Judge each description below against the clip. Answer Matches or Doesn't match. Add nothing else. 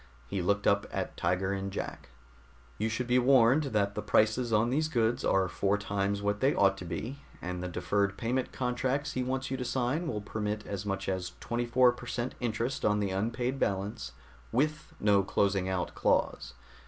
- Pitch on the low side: Matches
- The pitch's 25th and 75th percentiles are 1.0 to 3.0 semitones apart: Doesn't match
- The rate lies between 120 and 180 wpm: Doesn't match